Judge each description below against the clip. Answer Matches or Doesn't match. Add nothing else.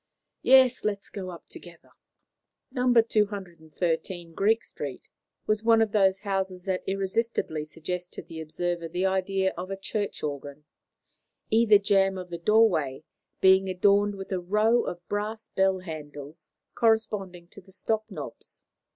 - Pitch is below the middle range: Doesn't match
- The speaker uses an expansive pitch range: Doesn't match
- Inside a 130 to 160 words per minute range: Matches